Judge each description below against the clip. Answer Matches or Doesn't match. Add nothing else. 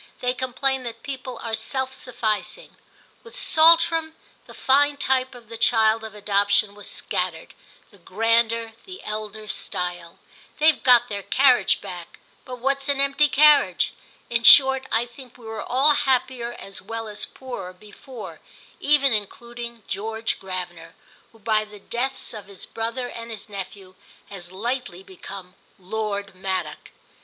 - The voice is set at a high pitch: Matches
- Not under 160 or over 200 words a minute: Doesn't match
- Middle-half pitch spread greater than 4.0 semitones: Matches